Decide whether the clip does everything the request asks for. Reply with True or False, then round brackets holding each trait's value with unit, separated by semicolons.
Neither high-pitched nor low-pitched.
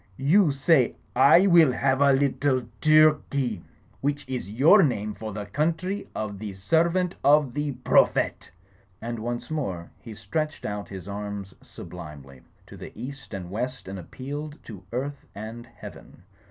False (130 Hz)